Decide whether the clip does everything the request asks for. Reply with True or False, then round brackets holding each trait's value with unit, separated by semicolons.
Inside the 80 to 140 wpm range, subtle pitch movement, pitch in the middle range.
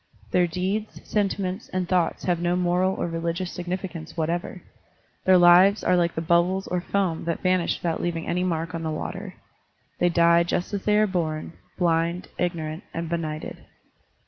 False (170 wpm; 1.7 semitones; 175 Hz)